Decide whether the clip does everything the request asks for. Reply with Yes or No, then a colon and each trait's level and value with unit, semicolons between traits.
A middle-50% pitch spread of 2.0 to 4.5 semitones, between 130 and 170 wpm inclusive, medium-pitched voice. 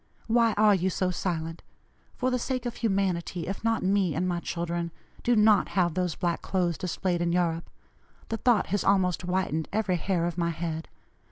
No: average, 3.1 semitones; average, 185 wpm; medium, 180 Hz